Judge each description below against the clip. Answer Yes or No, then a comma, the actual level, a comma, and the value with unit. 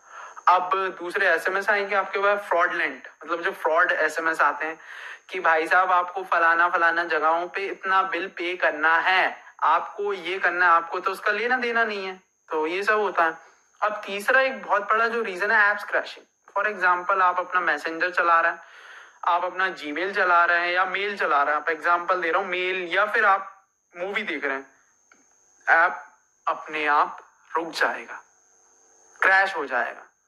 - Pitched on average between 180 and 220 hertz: Yes, medium, 185 Hz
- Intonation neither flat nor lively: Yes, average, 3.1 semitones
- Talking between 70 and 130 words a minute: No, fast, 190 wpm